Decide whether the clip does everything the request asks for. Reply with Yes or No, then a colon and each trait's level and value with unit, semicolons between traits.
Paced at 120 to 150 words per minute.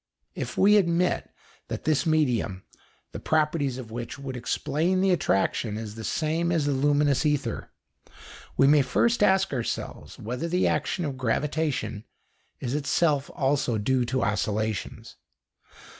Yes: average, 140 wpm